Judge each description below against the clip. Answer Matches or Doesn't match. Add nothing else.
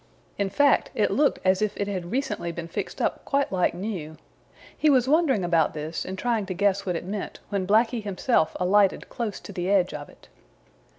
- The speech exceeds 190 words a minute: Matches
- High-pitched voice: Matches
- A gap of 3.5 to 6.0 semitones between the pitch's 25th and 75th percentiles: Matches